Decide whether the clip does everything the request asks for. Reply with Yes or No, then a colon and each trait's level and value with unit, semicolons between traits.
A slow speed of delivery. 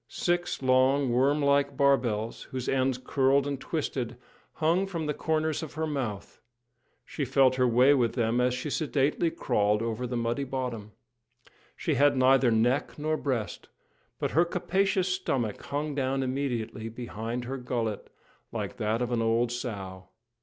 No: average, 155 wpm